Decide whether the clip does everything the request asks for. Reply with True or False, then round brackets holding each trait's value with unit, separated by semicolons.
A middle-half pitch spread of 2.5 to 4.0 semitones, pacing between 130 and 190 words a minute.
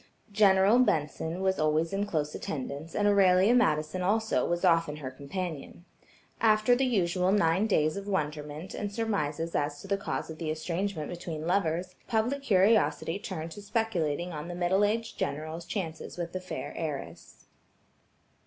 False (4.5 semitones; 155 wpm)